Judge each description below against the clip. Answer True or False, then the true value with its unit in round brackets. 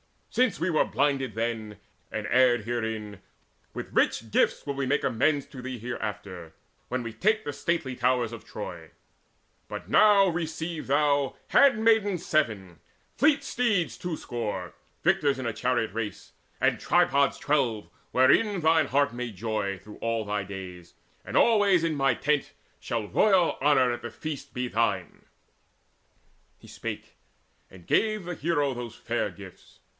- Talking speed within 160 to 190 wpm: False (150 wpm)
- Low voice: True (130 Hz)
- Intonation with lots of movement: True (6.4 semitones)